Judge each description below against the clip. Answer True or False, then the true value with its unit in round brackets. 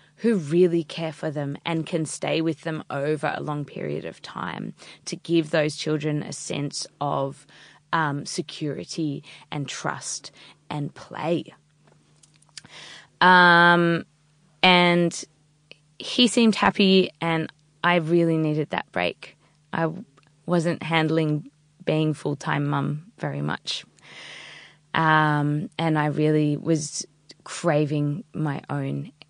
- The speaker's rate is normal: False (115 wpm)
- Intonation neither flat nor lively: False (2.1 semitones)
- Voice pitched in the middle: True (155 Hz)